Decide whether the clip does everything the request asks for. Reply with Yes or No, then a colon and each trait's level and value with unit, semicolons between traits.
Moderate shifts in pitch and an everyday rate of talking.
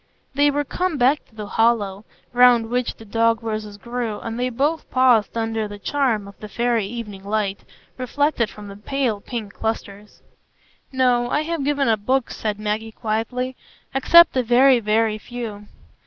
Yes: average, 3.2 semitones; average, 170 wpm